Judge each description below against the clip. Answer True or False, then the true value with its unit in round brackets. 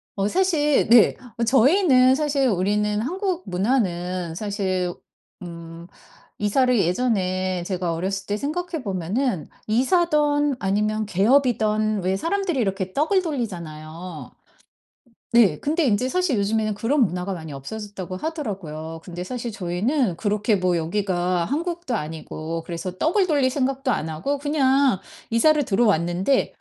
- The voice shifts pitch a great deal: True (6.9 semitones)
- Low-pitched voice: False (210 Hz)